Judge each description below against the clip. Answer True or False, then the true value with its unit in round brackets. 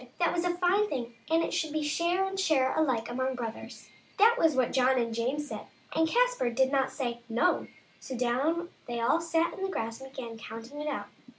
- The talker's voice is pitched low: False (275 Hz)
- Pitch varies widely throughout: True (5.9 semitones)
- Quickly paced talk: True (225 wpm)